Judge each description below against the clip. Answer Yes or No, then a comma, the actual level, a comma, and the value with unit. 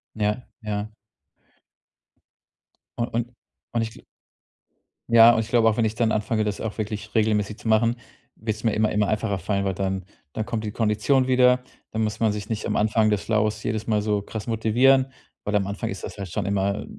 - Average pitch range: No, narrow, 1.5 semitones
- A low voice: Yes, low, 110 Hz